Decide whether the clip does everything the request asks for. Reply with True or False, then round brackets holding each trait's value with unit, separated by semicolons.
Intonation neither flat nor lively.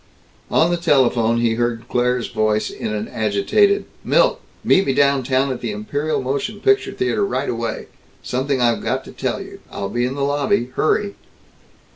True (4.0 semitones)